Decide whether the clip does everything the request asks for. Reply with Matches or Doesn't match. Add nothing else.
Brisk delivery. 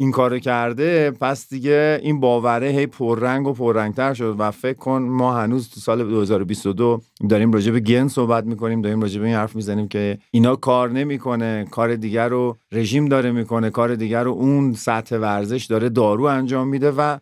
Matches